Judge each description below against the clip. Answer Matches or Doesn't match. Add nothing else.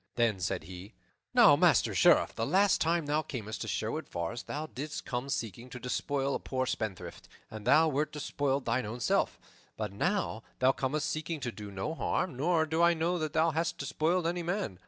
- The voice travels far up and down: Matches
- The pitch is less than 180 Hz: Matches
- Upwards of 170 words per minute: Matches